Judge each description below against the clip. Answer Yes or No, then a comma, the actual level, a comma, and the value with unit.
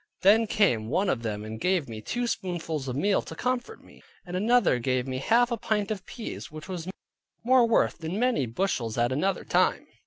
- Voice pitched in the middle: Yes, medium, 180 Hz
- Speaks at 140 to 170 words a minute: No, fast, 205 wpm